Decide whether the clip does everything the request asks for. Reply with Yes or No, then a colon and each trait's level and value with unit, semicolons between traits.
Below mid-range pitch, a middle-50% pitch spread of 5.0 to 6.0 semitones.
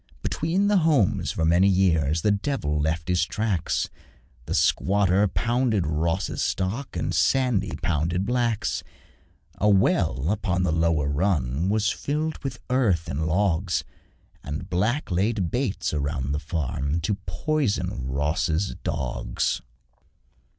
Yes: very low, 95 Hz; wide, 5.6 semitones